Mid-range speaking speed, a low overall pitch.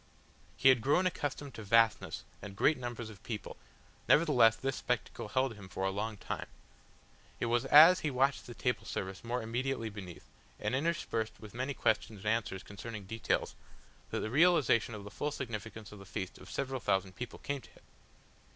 Yes: average, 185 wpm; low, 115 Hz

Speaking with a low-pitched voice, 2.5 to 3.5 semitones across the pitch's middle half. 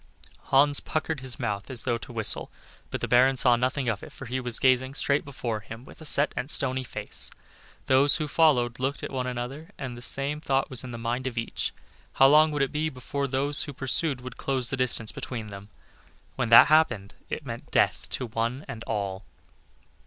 Yes: low, 130 Hz; average, 2.9 semitones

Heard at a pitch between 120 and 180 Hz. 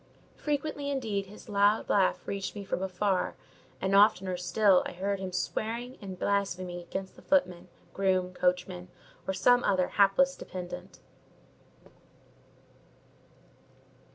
No: high, 195 Hz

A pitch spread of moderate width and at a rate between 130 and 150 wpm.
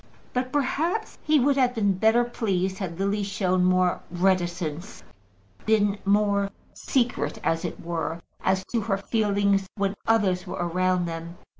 Yes: average, 3.5 semitones; average, 145 wpm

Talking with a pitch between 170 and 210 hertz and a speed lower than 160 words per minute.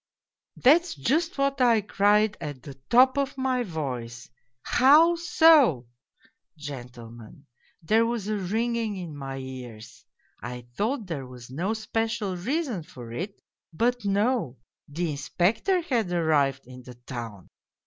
Yes: medium, 185 Hz; average, 140 wpm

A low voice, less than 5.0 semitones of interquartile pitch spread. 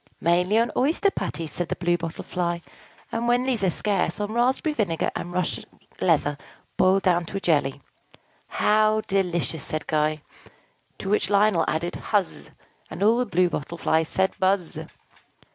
No: medium, 185 Hz; average, 4.3 semitones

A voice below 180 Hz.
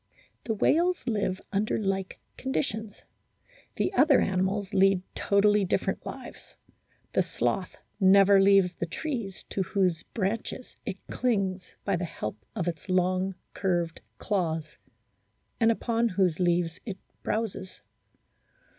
No: high, 195 Hz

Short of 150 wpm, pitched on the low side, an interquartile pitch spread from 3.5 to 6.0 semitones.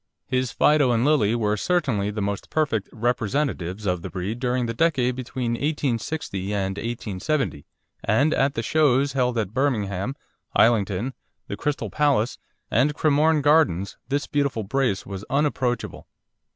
Yes: average, 140 wpm; low, 125 Hz; wide, 5.5 semitones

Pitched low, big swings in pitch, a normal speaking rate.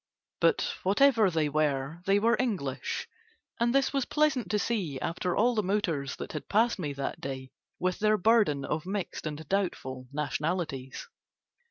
No: medium, 180 Hz; wide, 6.9 semitones; average, 160 wpm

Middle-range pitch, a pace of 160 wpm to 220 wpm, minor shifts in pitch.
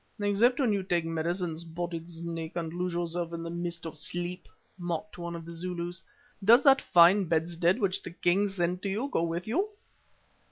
Yes: medium, 175 Hz; average, 185 wpm; narrow, 2.3 semitones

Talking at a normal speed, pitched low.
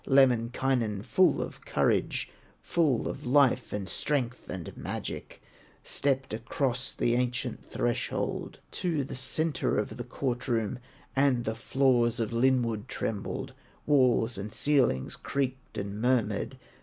No: slow, 125 wpm; low, 125 Hz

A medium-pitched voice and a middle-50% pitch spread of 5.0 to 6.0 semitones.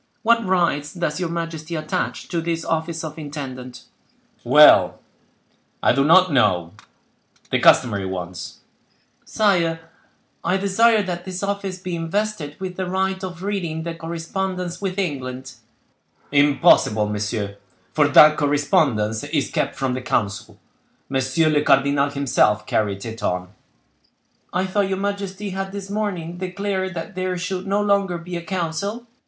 Yes: medium, 165 Hz; average, 5.3 semitones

